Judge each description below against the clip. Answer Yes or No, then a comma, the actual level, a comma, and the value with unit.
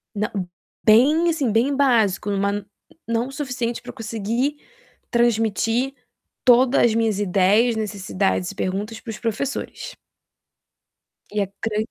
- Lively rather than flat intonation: No, average, 3.2 semitones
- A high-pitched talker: Yes, high, 225 Hz